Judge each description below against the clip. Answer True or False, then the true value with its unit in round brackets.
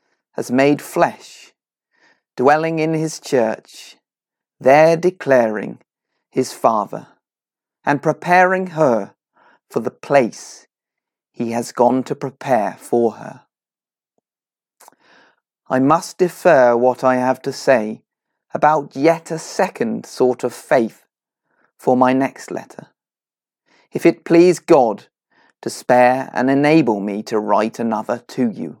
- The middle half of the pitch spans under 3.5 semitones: False (4.2 semitones)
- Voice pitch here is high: False (140 Hz)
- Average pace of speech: False (120 wpm)